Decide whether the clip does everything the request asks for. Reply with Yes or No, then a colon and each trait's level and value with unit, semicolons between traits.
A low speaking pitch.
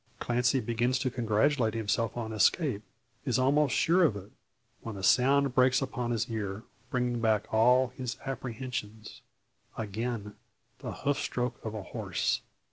Yes: low, 120 Hz